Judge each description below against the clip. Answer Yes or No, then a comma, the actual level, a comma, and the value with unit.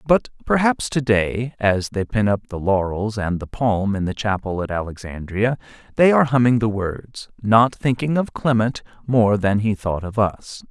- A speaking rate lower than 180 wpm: No, average, 185 wpm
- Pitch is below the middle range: Yes, low, 110 Hz